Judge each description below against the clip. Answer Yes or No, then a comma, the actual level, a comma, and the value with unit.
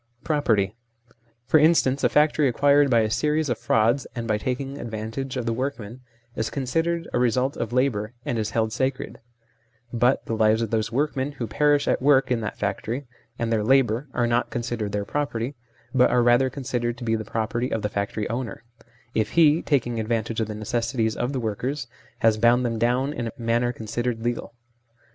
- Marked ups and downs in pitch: No, average, 3.1 semitones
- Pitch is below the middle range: Yes, low, 120 Hz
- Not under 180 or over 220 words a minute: Yes, average, 190 wpm